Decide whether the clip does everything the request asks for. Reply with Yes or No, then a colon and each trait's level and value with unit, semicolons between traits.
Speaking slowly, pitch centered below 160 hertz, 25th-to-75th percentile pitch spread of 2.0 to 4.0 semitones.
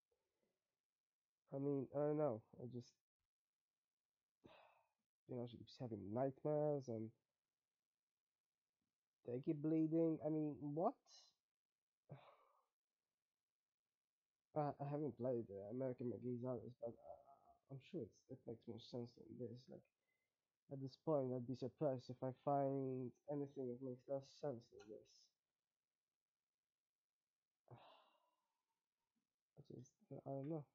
Yes: slow, 120 wpm; low, 135 Hz; average, 3.4 semitones